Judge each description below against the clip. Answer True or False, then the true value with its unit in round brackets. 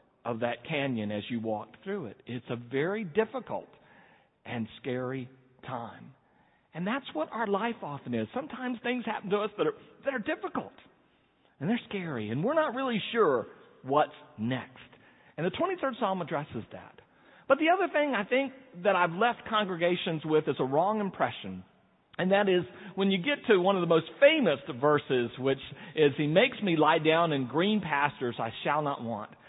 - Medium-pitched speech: True (180 Hz)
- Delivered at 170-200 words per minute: True (185 wpm)